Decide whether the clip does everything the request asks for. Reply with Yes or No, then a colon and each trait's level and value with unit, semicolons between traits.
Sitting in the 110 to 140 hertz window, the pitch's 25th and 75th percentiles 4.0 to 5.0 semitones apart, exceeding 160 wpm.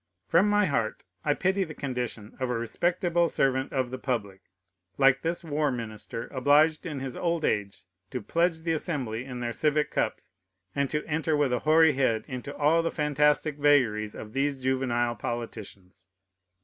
Yes: low, 135 Hz; average, 4.5 semitones; average, 170 wpm